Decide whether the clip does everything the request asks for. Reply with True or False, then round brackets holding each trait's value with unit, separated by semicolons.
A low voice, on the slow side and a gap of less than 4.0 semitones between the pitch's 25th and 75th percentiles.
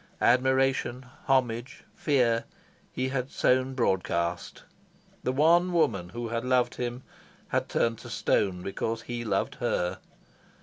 True (120 Hz; 125 wpm; 2.5 semitones)